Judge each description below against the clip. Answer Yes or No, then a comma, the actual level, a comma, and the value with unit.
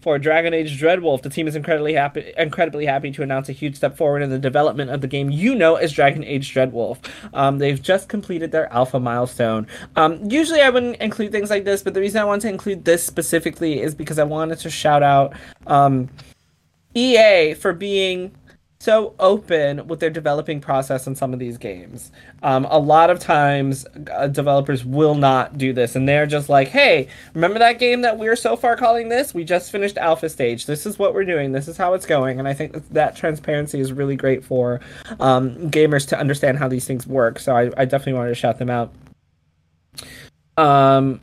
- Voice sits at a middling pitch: Yes, medium, 150 Hz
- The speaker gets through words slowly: No, fast, 205 wpm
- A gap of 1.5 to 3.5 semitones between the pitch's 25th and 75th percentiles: No, average, 4.4 semitones